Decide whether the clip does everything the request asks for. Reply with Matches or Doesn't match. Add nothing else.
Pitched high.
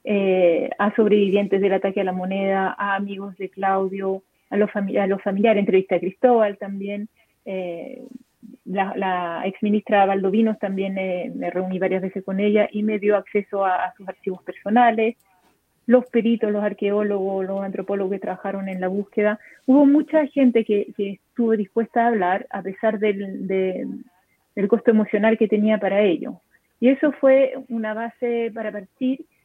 Matches